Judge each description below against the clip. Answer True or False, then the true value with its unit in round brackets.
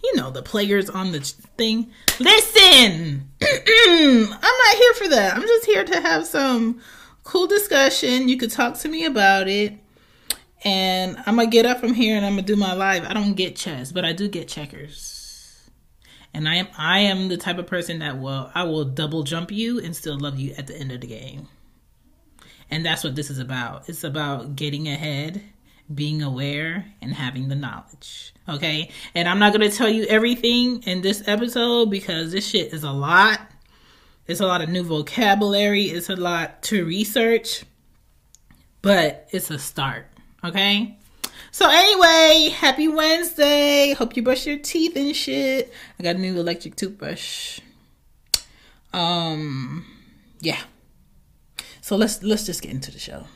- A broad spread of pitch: True (7.4 semitones)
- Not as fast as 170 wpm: False (175 wpm)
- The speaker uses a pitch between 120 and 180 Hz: False (190 Hz)